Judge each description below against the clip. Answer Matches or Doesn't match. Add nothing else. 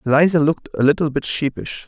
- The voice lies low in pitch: Doesn't match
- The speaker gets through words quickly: Doesn't match